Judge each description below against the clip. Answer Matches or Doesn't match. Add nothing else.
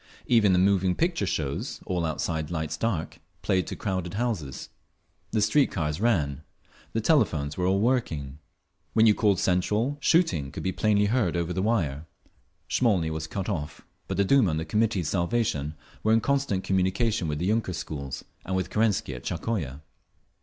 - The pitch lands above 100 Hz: Doesn't match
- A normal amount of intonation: Doesn't match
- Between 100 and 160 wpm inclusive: Doesn't match